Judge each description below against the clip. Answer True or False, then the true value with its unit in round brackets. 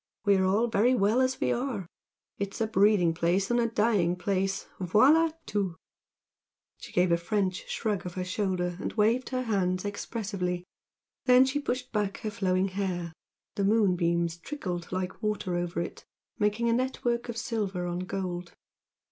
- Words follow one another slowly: False (165 wpm)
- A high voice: True (200 Hz)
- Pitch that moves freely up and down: False (4.1 semitones)